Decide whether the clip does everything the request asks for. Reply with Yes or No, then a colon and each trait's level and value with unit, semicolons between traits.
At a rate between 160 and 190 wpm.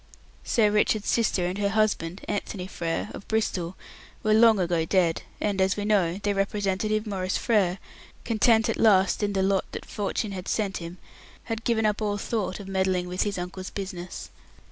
Yes: average, 180 wpm